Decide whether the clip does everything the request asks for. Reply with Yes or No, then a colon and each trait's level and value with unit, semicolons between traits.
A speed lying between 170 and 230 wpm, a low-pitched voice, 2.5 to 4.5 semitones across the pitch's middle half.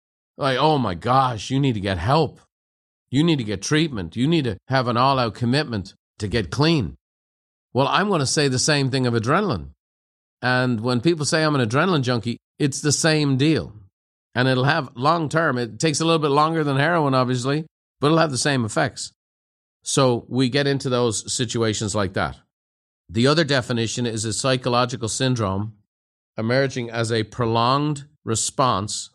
No: average, 175 wpm; low, 125 Hz; average, 5.3 semitones